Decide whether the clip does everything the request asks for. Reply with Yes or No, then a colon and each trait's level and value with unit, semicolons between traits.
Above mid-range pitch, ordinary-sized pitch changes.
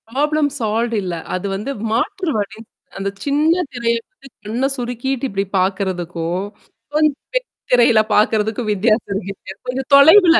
No: high, 235 Hz; wide, 5.9 semitones